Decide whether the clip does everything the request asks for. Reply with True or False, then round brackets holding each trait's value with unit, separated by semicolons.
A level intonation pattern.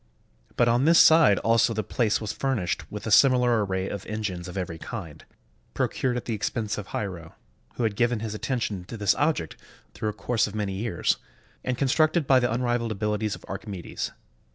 False (3.5 semitones)